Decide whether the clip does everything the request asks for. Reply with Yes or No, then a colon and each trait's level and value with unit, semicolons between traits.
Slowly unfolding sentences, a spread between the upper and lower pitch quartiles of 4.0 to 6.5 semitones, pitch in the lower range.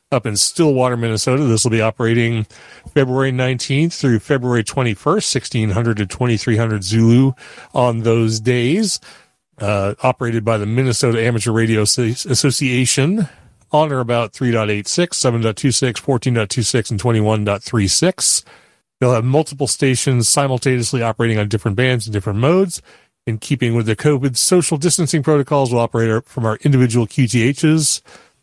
No: slow, 130 wpm; average, 3.2 semitones; low, 120 Hz